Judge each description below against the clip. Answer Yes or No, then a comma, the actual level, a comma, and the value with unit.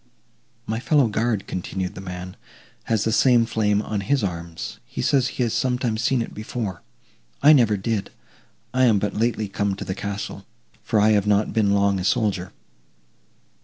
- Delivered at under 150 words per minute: No, average, 175 wpm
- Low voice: Yes, low, 105 Hz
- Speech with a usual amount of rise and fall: Yes, average, 3.0 semitones